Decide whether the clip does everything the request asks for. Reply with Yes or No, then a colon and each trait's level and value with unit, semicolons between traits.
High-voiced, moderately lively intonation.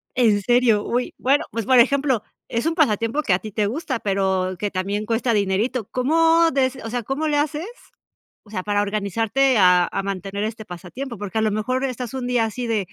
Yes: high, 225 Hz; average, 4.2 semitones